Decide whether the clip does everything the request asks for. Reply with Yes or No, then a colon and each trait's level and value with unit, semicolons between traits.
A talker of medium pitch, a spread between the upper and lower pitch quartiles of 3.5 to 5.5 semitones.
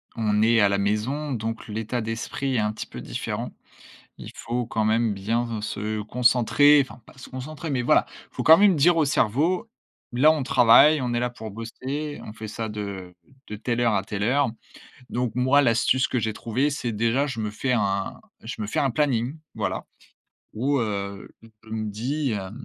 No: low, 115 Hz; average, 4.0 semitones